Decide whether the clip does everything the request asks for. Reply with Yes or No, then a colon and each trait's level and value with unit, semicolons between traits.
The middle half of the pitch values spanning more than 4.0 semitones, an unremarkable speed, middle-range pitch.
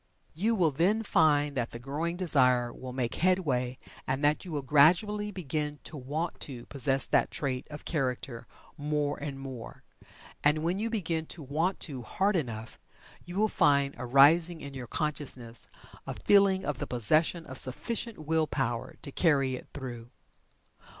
Yes: average, 4.5 semitones; average, 165 wpm; medium, 145 Hz